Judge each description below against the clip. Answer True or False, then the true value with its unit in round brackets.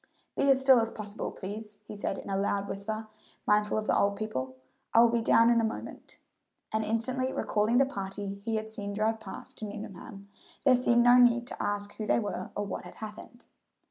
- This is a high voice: True (215 Hz)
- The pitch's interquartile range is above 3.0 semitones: False (2.5 semitones)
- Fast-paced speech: True (210 wpm)